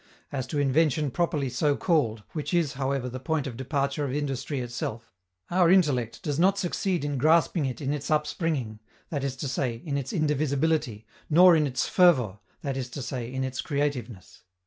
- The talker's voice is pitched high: No, medium, 140 Hz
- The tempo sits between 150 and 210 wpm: Yes, average, 185 wpm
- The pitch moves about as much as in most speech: Yes, average, 3.2 semitones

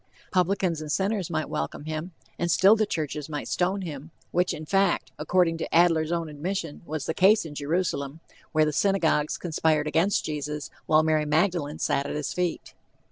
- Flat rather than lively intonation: No, average, 3.1 semitones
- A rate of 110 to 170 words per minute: No, average, 180 wpm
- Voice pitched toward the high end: No, medium, 160 Hz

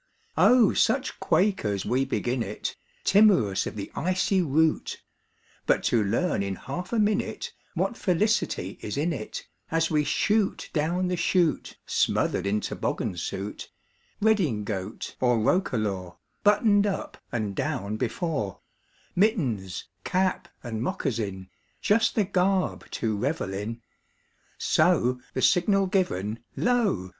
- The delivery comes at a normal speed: No, slow, 125 wpm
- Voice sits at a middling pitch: Yes, medium, 150 Hz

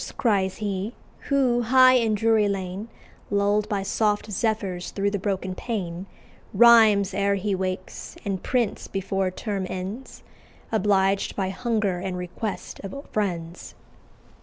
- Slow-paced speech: Yes, slow, 130 wpm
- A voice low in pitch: No, high, 200 Hz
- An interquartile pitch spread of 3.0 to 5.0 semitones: No, narrow, 2.6 semitones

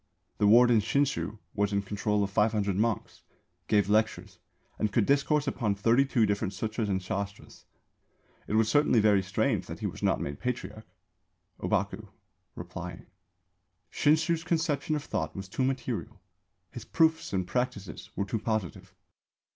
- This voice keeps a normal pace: Yes, average, 145 wpm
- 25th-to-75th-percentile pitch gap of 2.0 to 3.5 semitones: No, average, 4.3 semitones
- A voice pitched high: No, low, 110 Hz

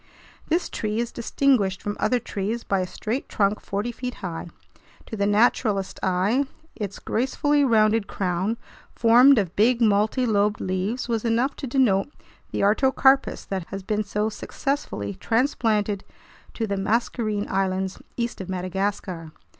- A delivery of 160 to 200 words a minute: No, average, 140 wpm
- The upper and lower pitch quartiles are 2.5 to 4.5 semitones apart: Yes, average, 3.5 semitones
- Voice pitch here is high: Yes, high, 215 Hz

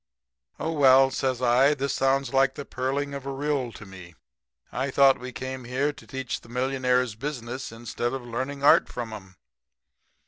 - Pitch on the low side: Yes, low, 130 Hz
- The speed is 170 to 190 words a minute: Yes, average, 175 wpm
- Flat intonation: Yes, narrow, 2.2 semitones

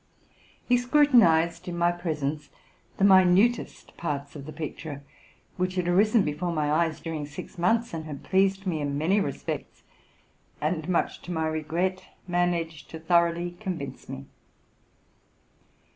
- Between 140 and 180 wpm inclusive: Yes, average, 145 wpm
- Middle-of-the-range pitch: Yes, medium, 170 Hz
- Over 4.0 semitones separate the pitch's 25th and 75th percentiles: No, average, 3.2 semitones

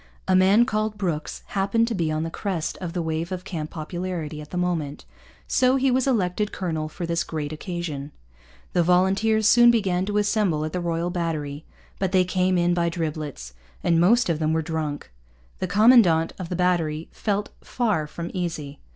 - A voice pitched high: No, medium, 175 Hz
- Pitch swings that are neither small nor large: Yes, average, 3.8 semitones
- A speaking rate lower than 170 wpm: No, average, 185 wpm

